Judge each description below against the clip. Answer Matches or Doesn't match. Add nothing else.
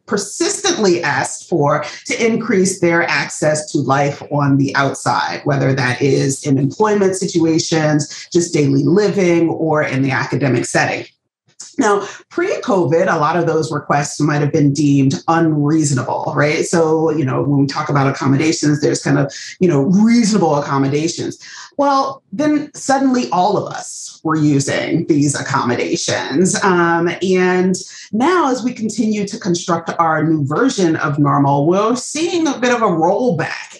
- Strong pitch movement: Matches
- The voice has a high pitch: Doesn't match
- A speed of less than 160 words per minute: Matches